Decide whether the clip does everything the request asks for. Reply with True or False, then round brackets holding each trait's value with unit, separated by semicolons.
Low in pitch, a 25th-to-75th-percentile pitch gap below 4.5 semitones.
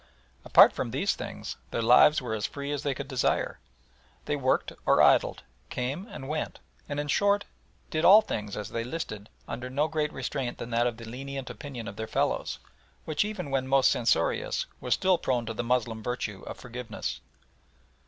True (130 Hz; 4.0 semitones)